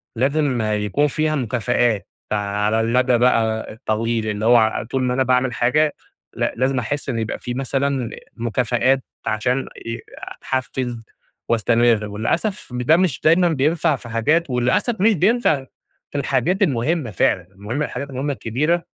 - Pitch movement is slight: No, average, 4.2 semitones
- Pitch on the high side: No, low, 125 Hz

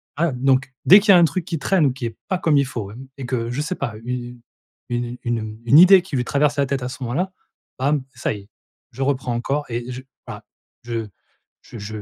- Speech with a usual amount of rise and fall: Yes, average, 3.7 semitones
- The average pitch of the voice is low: Yes, low, 130 Hz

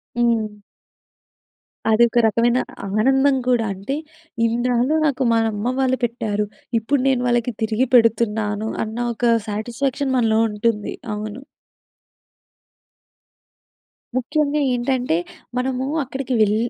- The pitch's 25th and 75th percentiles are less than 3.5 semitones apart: Yes, average, 3.0 semitones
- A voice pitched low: No, high, 235 Hz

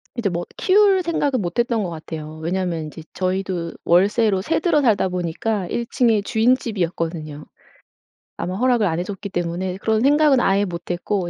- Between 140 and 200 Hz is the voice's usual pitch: Yes, high, 190 Hz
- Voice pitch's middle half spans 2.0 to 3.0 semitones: No, wide, 5.4 semitones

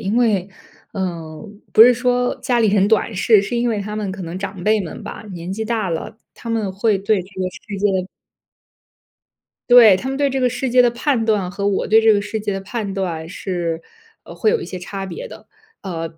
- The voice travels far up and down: No, average, 3.7 semitones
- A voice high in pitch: Yes, high, 205 Hz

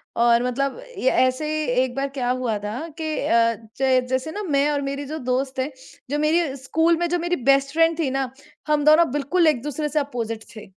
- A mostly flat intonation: No, average, 3.3 semitones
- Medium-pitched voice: No, very high, 275 Hz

